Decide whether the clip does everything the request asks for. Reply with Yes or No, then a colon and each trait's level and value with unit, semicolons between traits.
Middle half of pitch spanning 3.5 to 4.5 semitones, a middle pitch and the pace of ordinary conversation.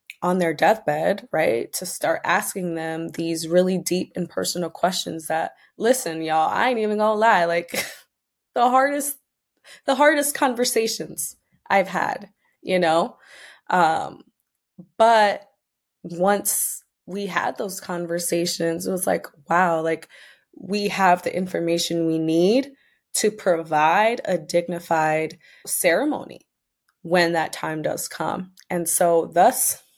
No: average, 4.2 semitones; medium, 180 Hz; slow, 125 wpm